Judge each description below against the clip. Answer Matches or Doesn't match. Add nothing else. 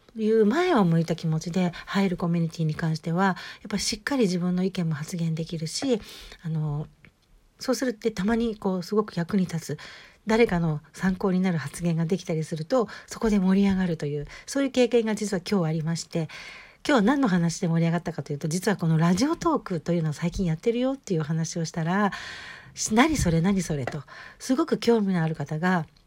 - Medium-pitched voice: Matches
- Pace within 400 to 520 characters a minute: Matches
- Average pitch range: Matches